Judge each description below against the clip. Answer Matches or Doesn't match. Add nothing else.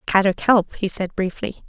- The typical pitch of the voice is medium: Doesn't match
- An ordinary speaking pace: Matches